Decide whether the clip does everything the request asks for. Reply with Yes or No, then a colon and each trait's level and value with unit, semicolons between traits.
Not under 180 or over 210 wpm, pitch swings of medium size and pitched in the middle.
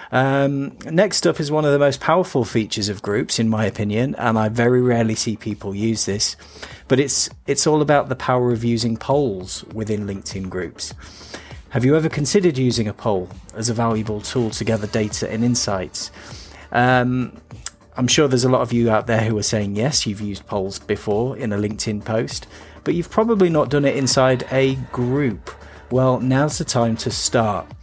No: average, 190 wpm; average, 4.0 semitones; low, 115 Hz